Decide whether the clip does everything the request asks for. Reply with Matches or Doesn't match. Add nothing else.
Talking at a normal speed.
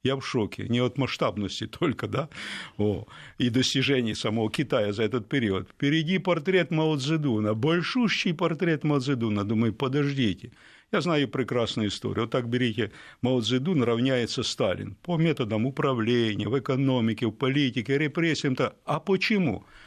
Matches